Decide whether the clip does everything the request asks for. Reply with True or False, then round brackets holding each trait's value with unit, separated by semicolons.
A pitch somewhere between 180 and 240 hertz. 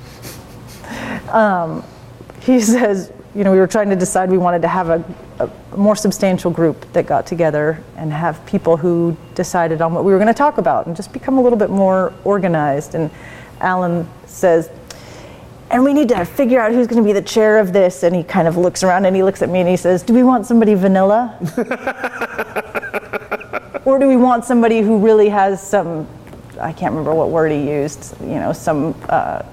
True (190 Hz)